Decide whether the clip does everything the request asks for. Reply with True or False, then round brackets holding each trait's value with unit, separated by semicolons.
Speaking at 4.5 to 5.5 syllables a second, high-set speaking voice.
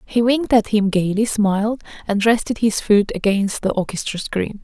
True (5.0 syllables/s; 210 Hz)